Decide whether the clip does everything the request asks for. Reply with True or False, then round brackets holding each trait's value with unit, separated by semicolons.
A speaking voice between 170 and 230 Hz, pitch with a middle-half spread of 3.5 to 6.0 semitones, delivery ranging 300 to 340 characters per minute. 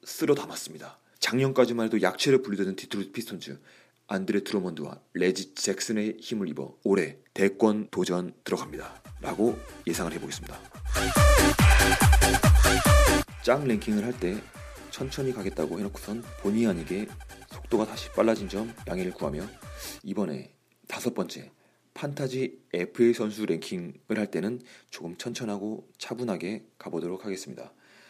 False (110 Hz; 5.1 semitones; 310 characters per minute)